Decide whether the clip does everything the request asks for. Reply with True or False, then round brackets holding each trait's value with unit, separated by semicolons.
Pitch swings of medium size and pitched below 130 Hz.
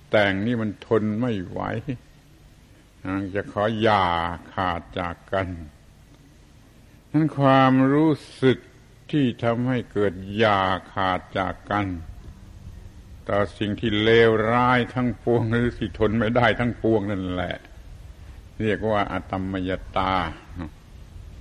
True (4.1 semitones; 100 Hz)